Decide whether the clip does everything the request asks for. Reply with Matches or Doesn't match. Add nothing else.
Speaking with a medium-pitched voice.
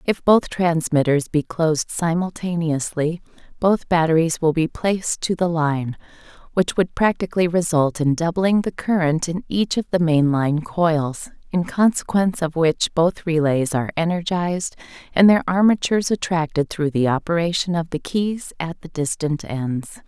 Matches